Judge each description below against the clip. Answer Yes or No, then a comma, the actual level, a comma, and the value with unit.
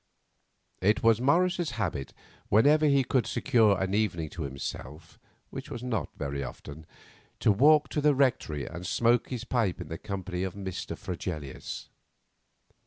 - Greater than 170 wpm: No, average, 150 wpm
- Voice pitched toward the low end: Yes, low, 105 Hz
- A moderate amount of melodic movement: No, wide, 6.9 semitones